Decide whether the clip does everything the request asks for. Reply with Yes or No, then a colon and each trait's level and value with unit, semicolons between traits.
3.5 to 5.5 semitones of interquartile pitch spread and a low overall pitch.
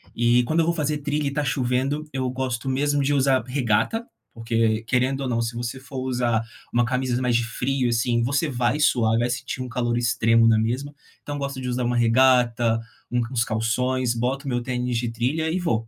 No: narrow, 2.5 semitones; low, 125 Hz